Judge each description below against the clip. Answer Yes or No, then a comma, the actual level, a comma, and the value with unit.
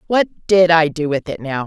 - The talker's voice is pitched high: No, medium, 165 Hz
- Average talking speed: No, fast, 255 wpm